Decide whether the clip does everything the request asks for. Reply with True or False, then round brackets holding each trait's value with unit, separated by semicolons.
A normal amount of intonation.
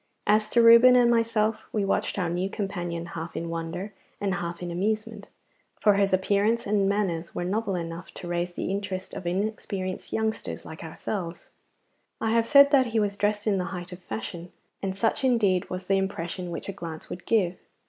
True (3.5 semitones)